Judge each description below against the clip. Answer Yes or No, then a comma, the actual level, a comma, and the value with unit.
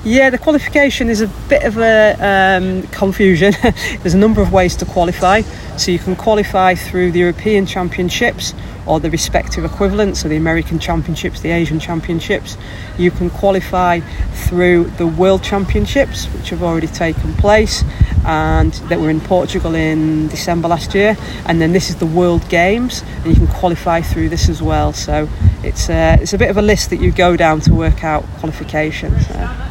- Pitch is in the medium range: Yes, medium, 175 Hz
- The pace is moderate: Yes, average, 180 wpm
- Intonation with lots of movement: No, average, 3.8 semitones